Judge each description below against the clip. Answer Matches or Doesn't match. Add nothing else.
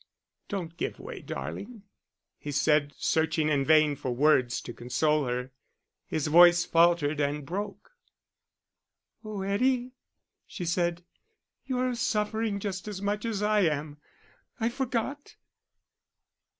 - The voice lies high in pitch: Doesn't match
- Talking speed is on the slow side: Matches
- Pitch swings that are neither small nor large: Doesn't match